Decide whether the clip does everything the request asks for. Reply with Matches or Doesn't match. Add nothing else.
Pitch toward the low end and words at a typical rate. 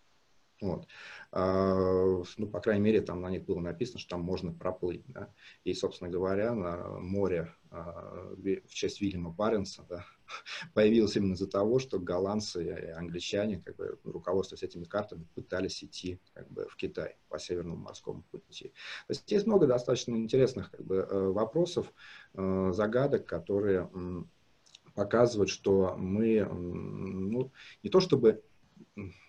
Matches